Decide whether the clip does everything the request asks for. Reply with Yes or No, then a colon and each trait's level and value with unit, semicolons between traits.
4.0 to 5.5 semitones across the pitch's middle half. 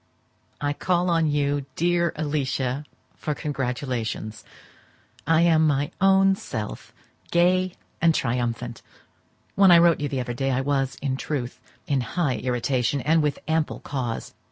Yes: average, 4.4 semitones